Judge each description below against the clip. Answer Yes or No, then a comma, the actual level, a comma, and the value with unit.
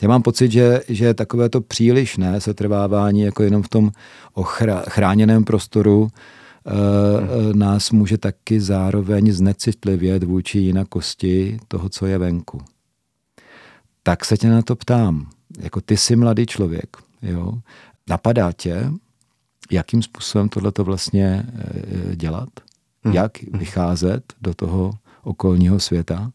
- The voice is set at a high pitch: No, low, 105 Hz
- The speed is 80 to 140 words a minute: Yes, average, 120 wpm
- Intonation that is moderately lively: Yes, average, 3.0 semitones